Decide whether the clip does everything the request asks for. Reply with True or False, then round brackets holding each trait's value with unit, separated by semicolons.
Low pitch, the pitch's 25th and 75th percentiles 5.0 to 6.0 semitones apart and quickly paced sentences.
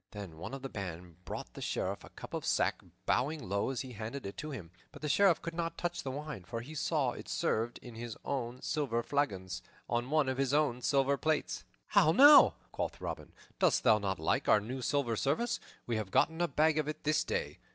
True (130 Hz; 5.4 semitones; 230 wpm)